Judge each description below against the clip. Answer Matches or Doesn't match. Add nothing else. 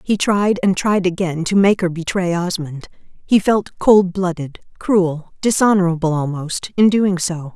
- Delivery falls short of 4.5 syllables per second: Matches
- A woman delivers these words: Matches